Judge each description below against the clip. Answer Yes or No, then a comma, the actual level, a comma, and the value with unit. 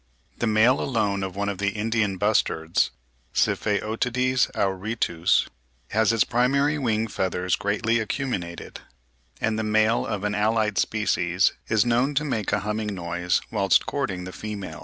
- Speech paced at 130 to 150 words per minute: Yes, average, 145 wpm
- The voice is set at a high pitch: No, low, 105 Hz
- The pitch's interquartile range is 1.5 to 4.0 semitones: Yes, average, 2.9 semitones